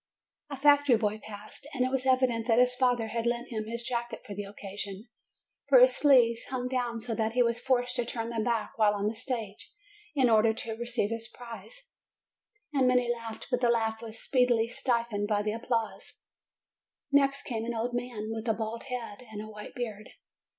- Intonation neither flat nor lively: No, narrow, 2.1 semitones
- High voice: Yes, high, 235 Hz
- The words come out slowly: No, average, 200 wpm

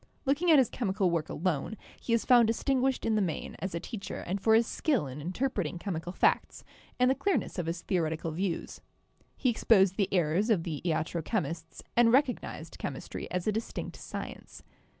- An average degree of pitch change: No, wide, 5.9 semitones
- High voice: Yes, high, 195 Hz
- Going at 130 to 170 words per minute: No, average, 190 wpm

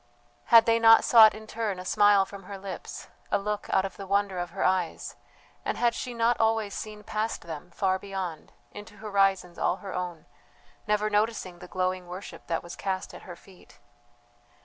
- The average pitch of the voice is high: Yes, high, 200 Hz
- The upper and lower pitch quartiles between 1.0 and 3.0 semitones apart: Yes, average, 2.7 semitones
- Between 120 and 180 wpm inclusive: No, average, 190 wpm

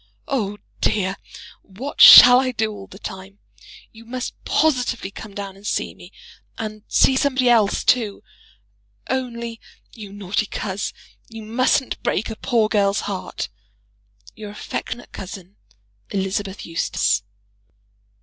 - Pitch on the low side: No, high, 215 Hz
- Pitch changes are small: No, average, 3.5 semitones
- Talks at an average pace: No, slow, 125 wpm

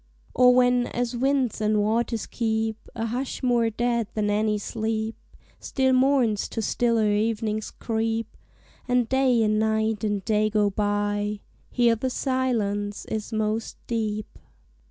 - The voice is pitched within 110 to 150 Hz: No, high, 225 Hz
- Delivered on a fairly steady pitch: Yes, narrow, 2.3 semitones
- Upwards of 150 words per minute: No, slow, 135 wpm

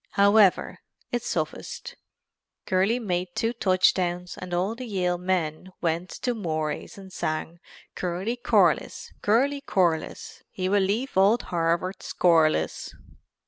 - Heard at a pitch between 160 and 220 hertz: Yes, medium, 185 Hz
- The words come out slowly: Yes, slow, 120 wpm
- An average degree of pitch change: Yes, average, 3.8 semitones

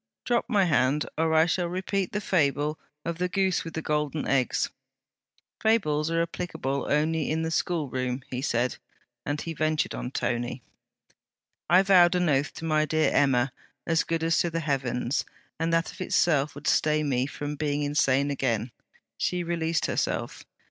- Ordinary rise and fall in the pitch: Yes, average, 3.2 semitones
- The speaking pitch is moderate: Yes, medium, 155 Hz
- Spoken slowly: No, average, 170 wpm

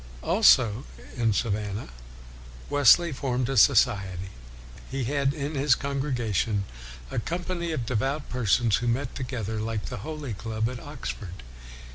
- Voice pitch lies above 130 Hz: No, low, 125 Hz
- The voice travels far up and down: No, average, 4.5 semitones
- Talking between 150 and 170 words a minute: No, slow, 135 wpm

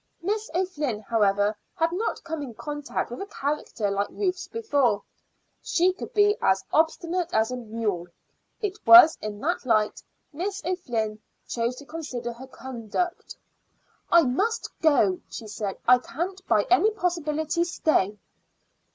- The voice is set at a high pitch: Yes, very high, 295 Hz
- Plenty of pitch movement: Yes, wide, 8.1 semitones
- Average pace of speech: Yes, average, 145 wpm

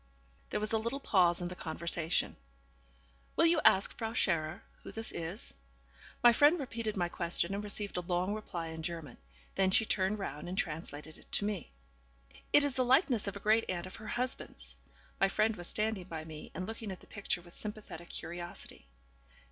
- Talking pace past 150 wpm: Yes, average, 190 wpm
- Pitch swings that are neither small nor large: Yes, average, 4.2 semitones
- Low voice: No, high, 195 Hz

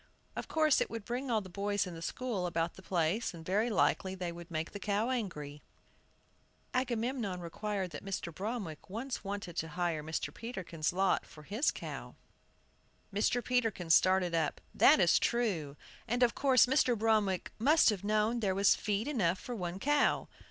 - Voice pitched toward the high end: Yes, high, 200 Hz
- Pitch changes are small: No, average, 5.2 semitones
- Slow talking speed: No, average, 175 wpm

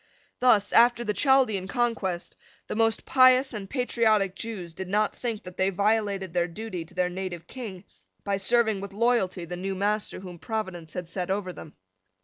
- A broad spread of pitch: No, average, 3.7 semitones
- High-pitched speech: Yes, high, 200 Hz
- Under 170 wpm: No, average, 175 wpm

